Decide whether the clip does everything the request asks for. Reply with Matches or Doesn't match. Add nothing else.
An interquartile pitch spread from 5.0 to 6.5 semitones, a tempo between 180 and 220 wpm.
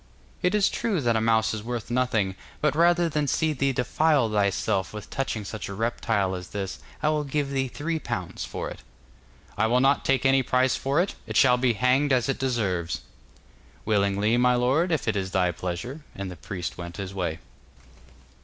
Matches